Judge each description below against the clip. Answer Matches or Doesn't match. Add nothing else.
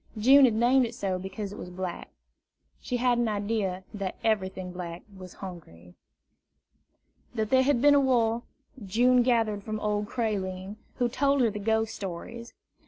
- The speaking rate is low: Doesn't match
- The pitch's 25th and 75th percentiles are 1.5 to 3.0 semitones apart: Doesn't match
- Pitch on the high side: Matches